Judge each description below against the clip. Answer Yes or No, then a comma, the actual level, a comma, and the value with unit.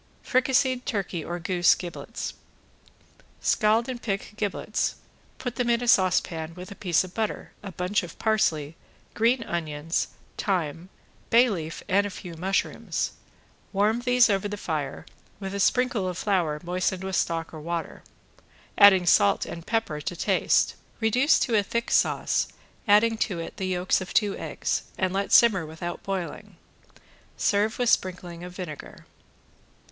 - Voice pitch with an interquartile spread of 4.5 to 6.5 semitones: No, average, 4.1 semitones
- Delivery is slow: No, average, 150 wpm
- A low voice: No, high, 190 Hz